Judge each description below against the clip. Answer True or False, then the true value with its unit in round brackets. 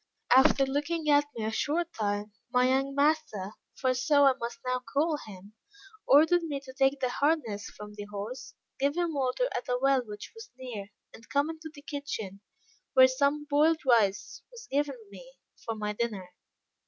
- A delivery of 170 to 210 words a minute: True (180 wpm)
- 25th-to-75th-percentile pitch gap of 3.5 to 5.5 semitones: True (4.8 semitones)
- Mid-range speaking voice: False (265 Hz)